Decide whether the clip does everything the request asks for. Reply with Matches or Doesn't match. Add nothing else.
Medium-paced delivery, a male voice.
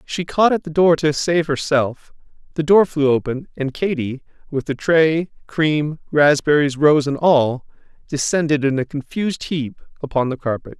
Matches